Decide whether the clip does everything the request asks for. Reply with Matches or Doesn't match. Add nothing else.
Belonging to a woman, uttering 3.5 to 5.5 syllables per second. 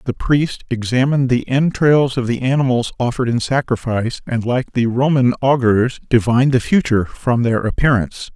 Doesn't match